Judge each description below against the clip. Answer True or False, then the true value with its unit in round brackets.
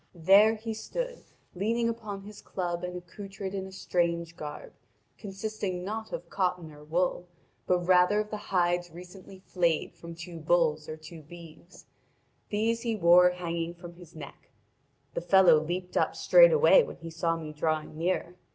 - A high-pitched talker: False (180 Hz)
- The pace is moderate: True (160 wpm)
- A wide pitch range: False (3.0 semitones)